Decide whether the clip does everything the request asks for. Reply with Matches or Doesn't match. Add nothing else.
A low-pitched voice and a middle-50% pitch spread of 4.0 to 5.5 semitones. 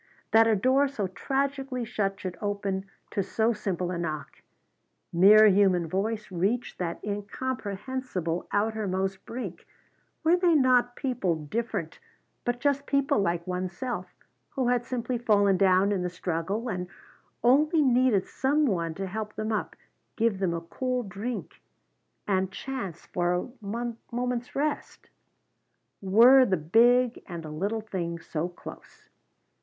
Doesn't match